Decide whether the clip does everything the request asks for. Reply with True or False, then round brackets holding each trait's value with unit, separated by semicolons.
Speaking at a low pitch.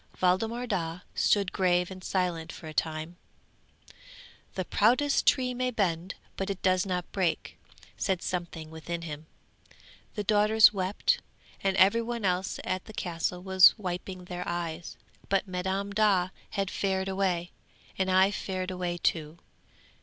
False (185 Hz)